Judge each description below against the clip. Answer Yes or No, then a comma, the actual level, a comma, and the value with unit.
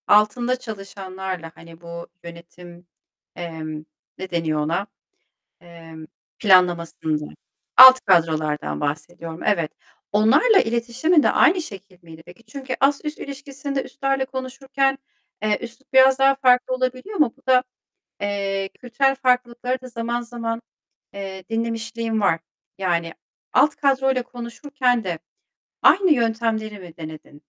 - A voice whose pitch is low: No, high, 225 Hz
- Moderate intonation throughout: No, wide, 6.9 semitones